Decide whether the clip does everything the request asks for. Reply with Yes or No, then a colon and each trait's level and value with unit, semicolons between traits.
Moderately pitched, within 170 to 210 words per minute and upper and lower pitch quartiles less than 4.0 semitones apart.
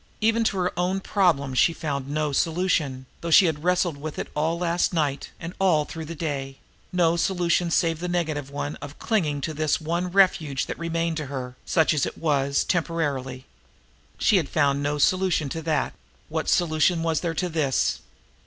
Yes: medium, 160 Hz; average, 190 wpm; average, 3.4 semitones